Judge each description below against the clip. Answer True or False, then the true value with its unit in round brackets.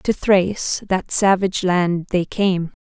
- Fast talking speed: False (150 wpm)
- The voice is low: False (185 Hz)